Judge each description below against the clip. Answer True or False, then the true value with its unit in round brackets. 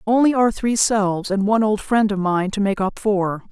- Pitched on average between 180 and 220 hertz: True (205 Hz)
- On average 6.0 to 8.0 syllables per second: False (5.1 syllables/s)